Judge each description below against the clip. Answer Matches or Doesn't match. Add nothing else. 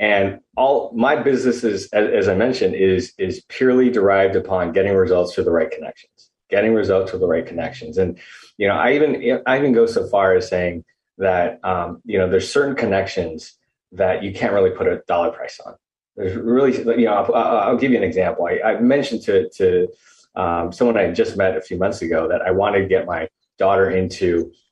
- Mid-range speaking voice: Doesn't match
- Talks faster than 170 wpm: Matches